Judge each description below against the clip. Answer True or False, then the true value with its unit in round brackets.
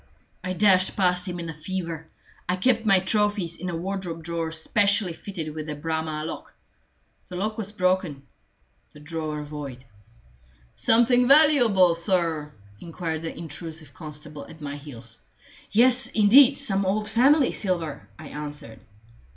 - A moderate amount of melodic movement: True (4.7 semitones)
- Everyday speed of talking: True (145 wpm)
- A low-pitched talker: False (175 Hz)